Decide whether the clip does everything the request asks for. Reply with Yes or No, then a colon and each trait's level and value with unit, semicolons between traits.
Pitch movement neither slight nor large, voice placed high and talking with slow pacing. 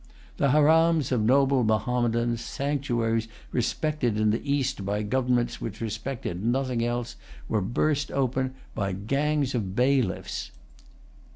No: average, 3.6 semitones; low, 125 Hz; slow, 120 wpm